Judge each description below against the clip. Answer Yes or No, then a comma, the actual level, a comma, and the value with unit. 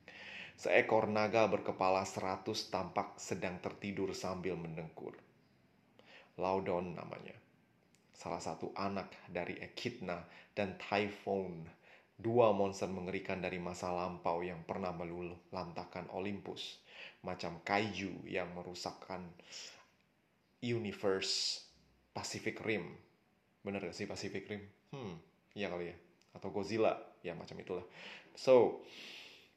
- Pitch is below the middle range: Yes, very low, 95 Hz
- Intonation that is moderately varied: No, narrow, 2.2 semitones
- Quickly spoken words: No, average, 100 wpm